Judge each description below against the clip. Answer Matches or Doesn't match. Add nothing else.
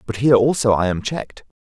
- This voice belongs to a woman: Doesn't match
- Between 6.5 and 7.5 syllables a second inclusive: Matches